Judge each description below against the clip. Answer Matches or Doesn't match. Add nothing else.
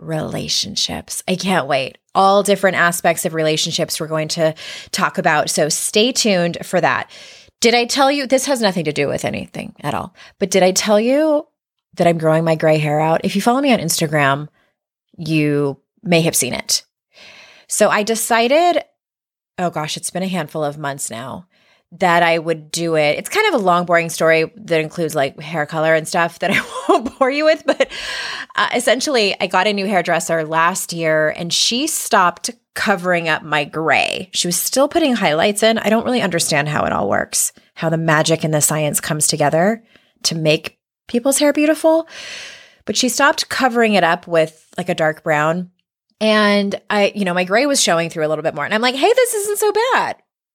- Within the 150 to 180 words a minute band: Doesn't match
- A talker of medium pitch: Matches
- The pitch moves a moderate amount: Doesn't match